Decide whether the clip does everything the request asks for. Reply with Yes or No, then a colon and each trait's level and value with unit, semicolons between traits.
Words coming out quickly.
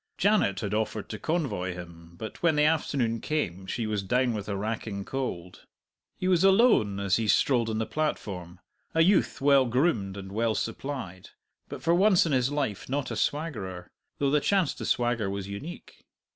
No: average, 185 wpm